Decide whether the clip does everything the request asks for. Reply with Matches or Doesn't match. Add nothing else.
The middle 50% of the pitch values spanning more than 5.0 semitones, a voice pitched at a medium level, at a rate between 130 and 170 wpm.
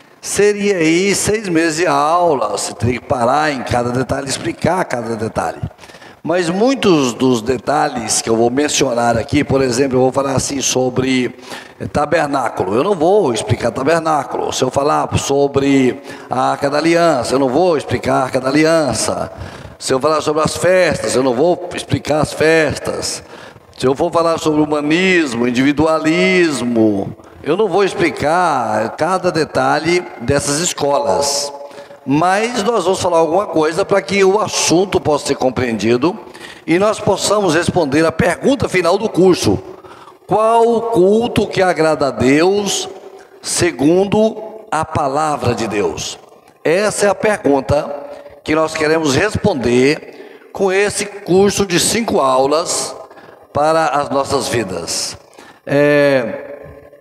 Matches